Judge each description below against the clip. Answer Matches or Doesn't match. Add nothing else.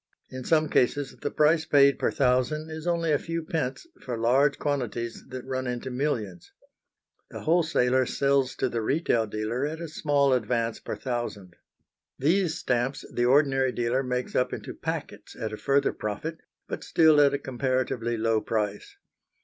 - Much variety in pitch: Doesn't match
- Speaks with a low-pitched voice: Matches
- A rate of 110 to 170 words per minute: Matches